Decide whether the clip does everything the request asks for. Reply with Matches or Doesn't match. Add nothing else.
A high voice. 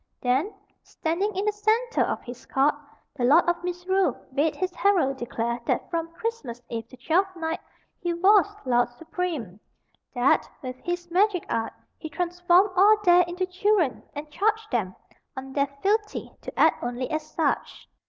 Matches